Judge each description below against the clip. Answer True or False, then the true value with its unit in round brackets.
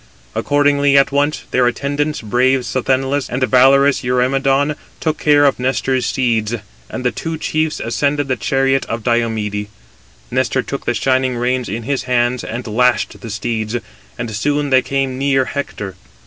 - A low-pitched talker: True (130 Hz)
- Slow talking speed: False (155 wpm)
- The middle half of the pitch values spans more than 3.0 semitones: False (2.6 semitones)